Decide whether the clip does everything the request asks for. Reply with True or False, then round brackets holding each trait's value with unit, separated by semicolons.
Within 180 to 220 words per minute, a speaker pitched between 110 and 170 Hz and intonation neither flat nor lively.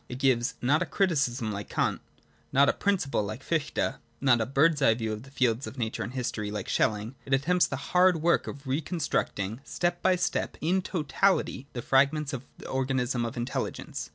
True (200 wpm; 135 Hz; 4.9 semitones)